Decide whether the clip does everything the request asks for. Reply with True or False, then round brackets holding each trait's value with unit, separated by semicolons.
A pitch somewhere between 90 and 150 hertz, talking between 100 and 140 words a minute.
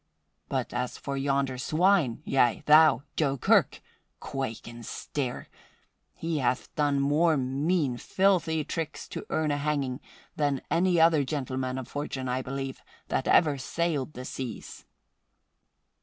True (140 Hz; 135 wpm)